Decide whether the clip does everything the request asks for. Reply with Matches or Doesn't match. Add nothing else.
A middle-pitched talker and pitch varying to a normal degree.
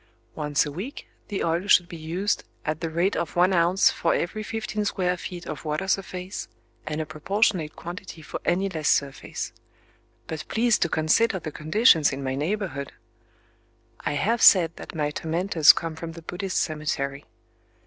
Matches